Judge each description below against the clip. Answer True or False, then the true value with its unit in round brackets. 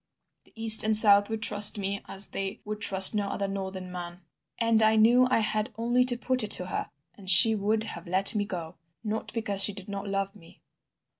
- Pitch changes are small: True (2.1 semitones)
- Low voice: False (205 Hz)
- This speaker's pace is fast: True (215 wpm)